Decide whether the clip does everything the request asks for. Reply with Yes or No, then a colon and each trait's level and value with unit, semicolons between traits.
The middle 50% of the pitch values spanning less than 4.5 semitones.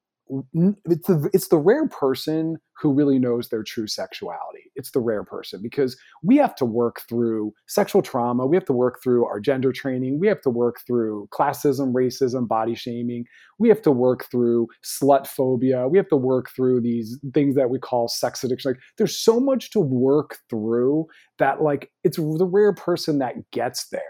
No: average, 4.9 semitones